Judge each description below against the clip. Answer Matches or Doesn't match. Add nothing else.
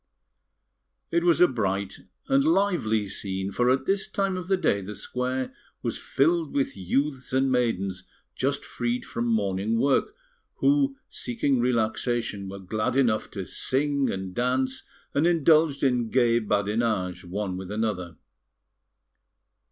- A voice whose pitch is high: Doesn't match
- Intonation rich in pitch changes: Matches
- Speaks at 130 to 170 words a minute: Matches